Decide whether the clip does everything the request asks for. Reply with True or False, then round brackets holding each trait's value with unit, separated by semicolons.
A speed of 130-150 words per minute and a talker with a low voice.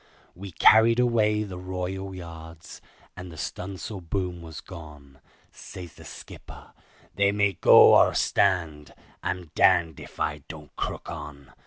True (140 wpm; 90 Hz)